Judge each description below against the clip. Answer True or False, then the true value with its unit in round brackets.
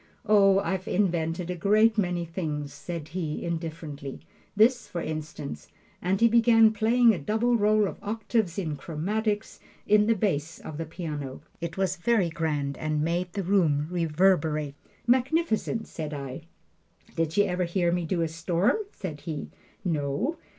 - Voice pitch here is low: False (175 Hz)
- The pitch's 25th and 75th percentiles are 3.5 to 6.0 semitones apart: True (4.9 semitones)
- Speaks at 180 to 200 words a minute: False (155 wpm)